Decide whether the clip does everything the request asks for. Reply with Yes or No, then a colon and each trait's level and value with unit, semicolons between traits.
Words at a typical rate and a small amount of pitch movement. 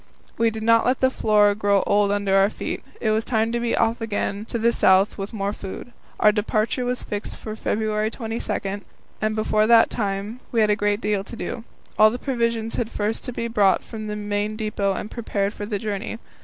No: fast, 215 wpm; narrow, 1.9 semitones